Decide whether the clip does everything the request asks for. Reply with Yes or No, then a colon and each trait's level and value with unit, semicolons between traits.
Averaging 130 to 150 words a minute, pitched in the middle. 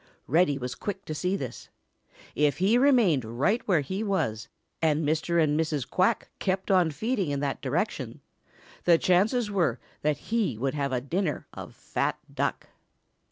No: average, 160 wpm; medium, 165 Hz